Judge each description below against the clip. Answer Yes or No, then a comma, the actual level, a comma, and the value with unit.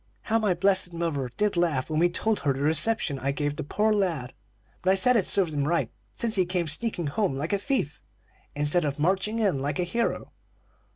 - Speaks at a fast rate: Yes, fast, 215 wpm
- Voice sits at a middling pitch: Yes, medium, 175 Hz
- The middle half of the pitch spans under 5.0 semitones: No, wide, 5.6 semitones